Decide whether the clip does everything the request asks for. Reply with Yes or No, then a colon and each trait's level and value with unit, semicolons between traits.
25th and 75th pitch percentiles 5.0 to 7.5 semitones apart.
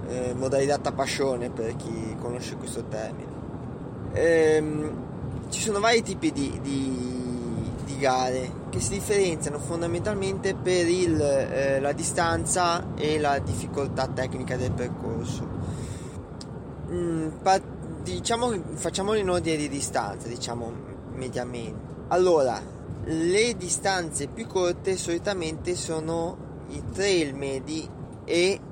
Yes: average, 5.3 semitones